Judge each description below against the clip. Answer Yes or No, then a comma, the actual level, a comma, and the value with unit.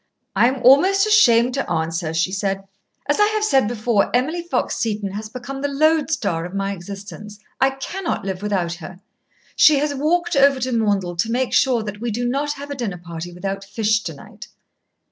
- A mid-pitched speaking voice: No, high, 230 Hz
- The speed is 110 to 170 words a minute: No, average, 195 wpm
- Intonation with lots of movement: Yes, wide, 6.1 semitones